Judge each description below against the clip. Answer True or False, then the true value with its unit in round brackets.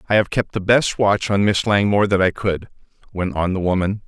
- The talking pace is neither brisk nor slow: False (235 wpm)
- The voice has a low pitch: True (100 Hz)